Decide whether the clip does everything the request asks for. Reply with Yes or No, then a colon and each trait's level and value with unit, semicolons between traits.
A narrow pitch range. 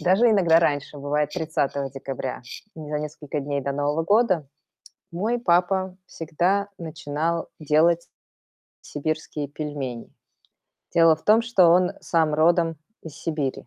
No: average, 3.2 semitones